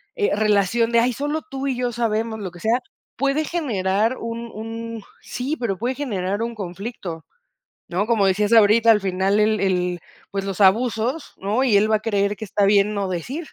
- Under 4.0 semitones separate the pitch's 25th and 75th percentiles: Yes, average, 3.1 semitones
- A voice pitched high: Yes, high, 215 Hz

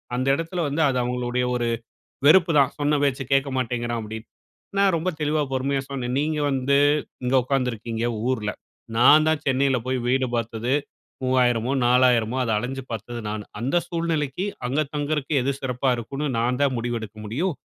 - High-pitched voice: No, low, 130 Hz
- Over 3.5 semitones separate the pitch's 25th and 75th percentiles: No, average, 3.2 semitones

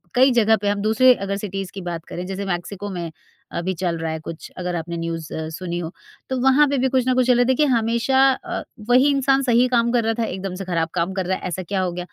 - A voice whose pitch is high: Yes, high, 200 Hz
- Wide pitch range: Yes, wide, 6.0 semitones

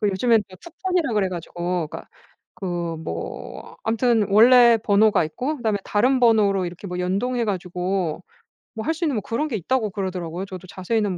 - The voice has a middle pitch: No, high, 205 Hz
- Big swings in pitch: No, average, 4.5 semitones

